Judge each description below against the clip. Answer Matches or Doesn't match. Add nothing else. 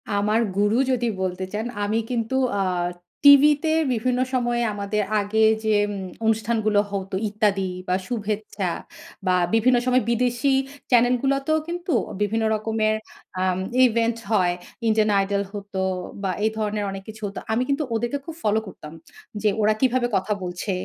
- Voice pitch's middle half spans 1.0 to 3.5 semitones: Matches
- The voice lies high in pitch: Matches